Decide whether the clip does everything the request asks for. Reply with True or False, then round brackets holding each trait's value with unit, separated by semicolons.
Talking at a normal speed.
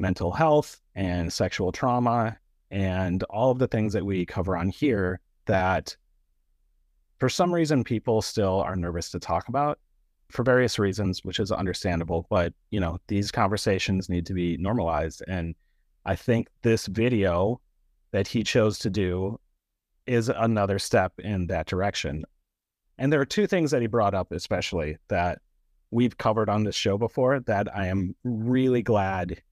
True (160 wpm)